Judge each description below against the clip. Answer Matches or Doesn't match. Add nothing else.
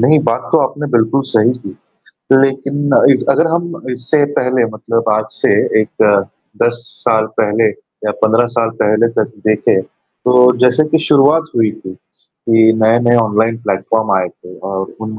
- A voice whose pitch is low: Matches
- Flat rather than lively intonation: Doesn't match